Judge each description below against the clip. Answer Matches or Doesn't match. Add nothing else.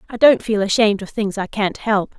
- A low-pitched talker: Doesn't match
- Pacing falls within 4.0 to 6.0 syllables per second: Matches